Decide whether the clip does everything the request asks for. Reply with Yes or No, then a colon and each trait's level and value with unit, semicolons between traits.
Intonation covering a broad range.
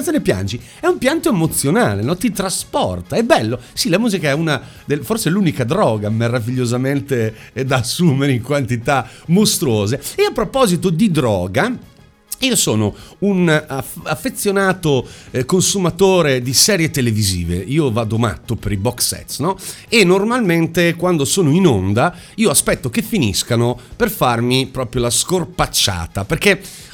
Yes: wide, 7.5 semitones